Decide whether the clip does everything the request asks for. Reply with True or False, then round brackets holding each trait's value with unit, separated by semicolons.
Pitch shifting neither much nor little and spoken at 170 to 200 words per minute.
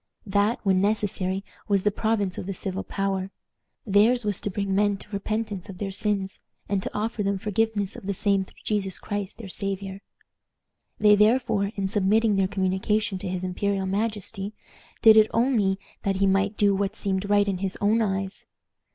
False (1.5 semitones; 180 wpm)